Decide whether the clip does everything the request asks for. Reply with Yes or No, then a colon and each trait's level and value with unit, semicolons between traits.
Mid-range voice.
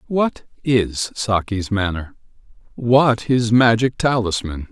No: low, 110 Hz